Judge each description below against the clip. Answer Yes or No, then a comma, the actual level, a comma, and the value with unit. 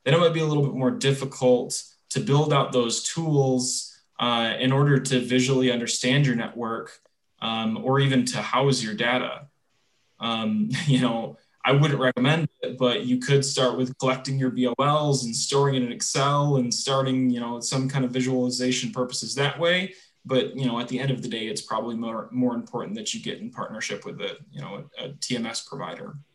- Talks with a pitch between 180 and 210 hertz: No, low, 130 Hz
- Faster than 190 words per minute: Yes, average, 200 wpm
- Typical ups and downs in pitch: No, narrow, 2.2 semitones